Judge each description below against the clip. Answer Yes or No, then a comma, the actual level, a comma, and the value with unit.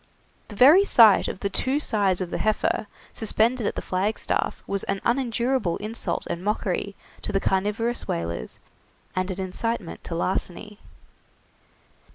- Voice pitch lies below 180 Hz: No, high, 205 Hz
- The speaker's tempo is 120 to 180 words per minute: Yes, average, 145 wpm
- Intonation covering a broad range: No, average, 3.7 semitones